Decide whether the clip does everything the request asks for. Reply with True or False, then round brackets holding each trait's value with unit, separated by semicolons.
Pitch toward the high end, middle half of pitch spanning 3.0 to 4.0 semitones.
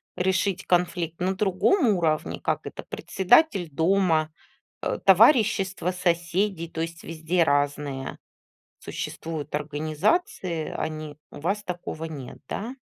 False (175 Hz; 3.5 semitones)